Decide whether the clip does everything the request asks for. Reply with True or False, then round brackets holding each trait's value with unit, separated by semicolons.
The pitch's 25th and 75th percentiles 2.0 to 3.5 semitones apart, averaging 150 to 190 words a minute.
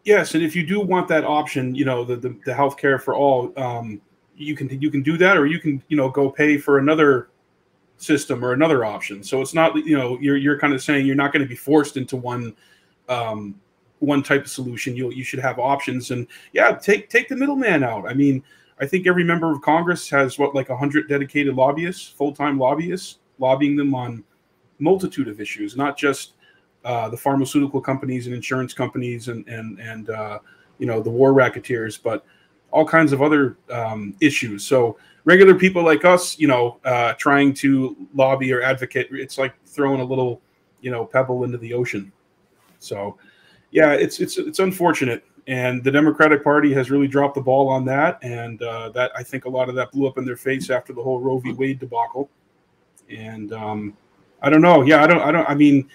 False (2.9 semitones; 205 wpm)